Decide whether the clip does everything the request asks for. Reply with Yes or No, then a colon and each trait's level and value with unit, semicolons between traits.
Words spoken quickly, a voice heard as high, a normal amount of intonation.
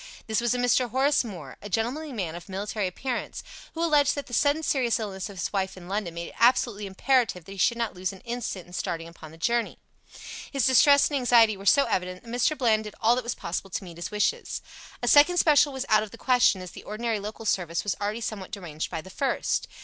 Yes: fast, 240 wpm; high, 220 Hz; average, 4.9 semitones